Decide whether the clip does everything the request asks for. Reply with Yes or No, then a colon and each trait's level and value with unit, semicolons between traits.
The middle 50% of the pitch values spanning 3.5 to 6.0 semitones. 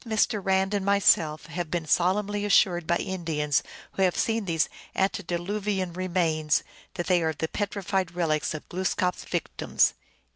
No: average, 3.0 semitones